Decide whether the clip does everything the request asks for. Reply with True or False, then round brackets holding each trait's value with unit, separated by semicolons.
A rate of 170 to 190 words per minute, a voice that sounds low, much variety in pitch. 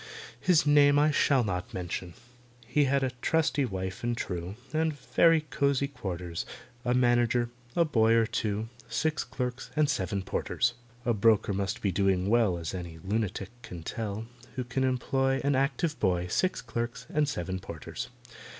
False (160 wpm; 120 Hz; 6.5 semitones)